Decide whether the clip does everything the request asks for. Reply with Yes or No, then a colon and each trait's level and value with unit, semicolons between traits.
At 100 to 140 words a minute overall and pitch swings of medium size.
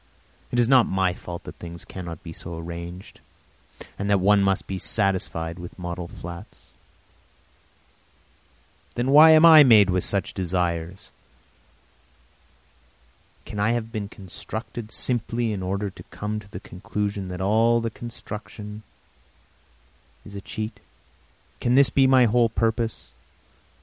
Yes: slow, 135 wpm; average, 4.0 semitones